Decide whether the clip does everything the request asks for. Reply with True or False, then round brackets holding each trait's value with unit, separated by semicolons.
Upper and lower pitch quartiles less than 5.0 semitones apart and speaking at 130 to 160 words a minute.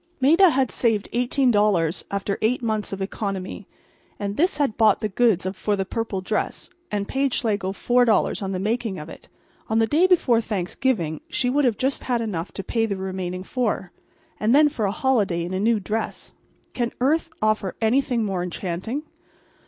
False (4.4 semitones; 175 wpm)